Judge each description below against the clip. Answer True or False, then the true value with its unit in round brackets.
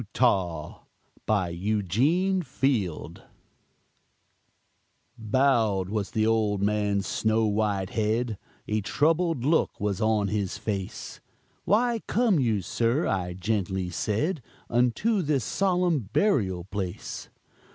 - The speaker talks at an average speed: False (105 wpm)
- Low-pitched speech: True (110 Hz)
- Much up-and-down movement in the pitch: True (5.9 semitones)